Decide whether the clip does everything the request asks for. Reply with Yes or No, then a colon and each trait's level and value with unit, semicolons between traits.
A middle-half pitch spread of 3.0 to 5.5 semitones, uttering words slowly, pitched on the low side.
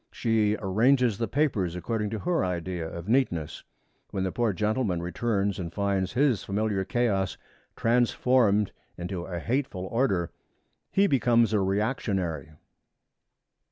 Yes: average, 4.4 semitones; slow, 125 wpm; low, 105 Hz